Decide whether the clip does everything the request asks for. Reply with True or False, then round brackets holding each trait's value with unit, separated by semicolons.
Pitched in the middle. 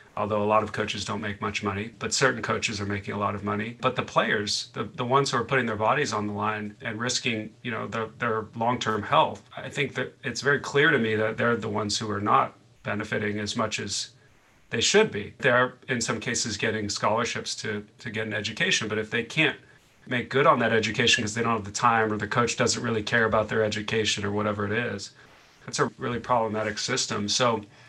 False (110 Hz)